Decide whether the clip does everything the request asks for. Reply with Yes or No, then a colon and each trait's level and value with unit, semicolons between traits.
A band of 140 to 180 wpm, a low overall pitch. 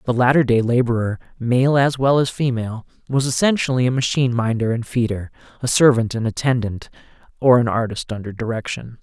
Yes: average, 165 wpm; low, 120 Hz